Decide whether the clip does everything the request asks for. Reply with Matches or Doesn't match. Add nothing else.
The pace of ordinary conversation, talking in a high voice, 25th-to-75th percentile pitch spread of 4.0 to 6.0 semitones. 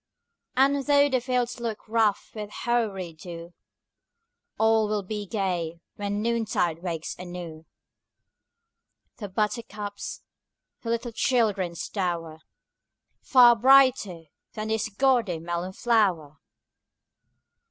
Doesn't match